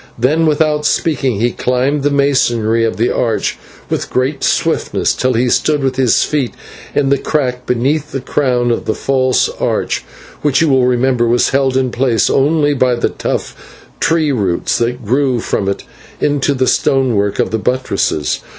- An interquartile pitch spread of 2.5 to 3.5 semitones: Yes, average, 2.9 semitones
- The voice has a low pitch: Yes, low, 130 Hz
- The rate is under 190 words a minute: Yes, average, 170 wpm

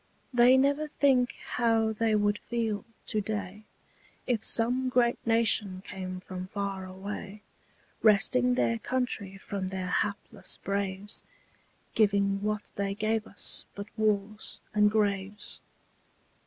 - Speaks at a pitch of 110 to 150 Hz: No, high, 205 Hz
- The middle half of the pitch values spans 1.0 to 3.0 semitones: Yes, narrow, 2.4 semitones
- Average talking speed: No, slow, 120 wpm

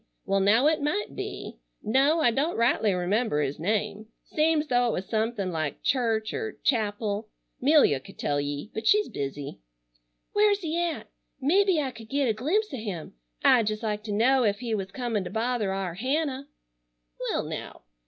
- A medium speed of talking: Yes, average, 180 wpm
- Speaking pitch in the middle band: No, high, 225 Hz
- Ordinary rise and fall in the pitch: No, wide, 5.9 semitones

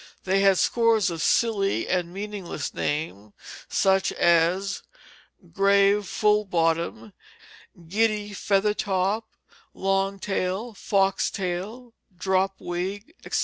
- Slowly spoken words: Yes, slow, 105 wpm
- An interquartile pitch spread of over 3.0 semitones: No, narrow, 2.5 semitones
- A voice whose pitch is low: No, high, 195 Hz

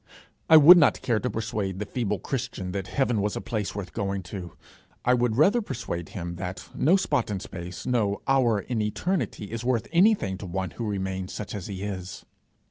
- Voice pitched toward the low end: Yes, low, 105 Hz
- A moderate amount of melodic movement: Yes, average, 4.7 semitones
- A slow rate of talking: No, average, 200 wpm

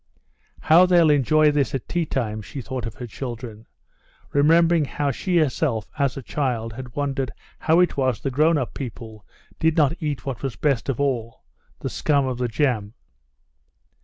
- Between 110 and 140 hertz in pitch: Yes, low, 135 Hz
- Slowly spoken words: No, average, 170 wpm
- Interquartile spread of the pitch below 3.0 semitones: No, average, 4.1 semitones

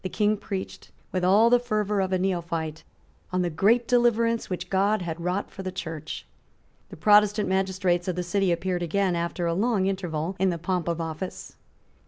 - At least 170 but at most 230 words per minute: Yes, average, 185 wpm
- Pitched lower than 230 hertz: Yes, medium, 185 Hz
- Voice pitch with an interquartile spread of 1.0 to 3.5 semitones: Yes, average, 2.9 semitones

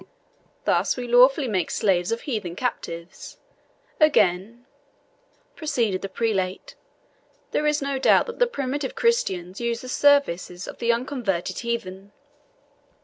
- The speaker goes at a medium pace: No, slow, 125 wpm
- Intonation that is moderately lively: No, wide, 6.6 semitones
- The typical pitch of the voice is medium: No, high, 235 Hz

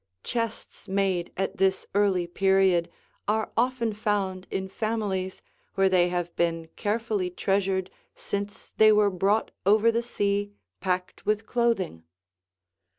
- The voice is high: Yes, high, 195 Hz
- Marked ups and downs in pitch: No, narrow, 2.5 semitones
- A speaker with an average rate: No, slow, 125 wpm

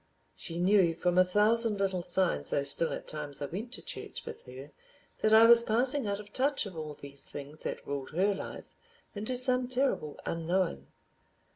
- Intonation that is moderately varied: No, wide, 6.4 semitones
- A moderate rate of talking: Yes, average, 175 wpm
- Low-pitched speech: No, high, 190 Hz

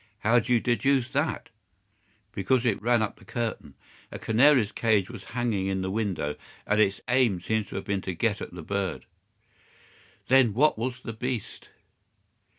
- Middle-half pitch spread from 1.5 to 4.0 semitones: Yes, average, 3.7 semitones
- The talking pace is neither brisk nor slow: Yes, average, 170 wpm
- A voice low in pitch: Yes, low, 110 Hz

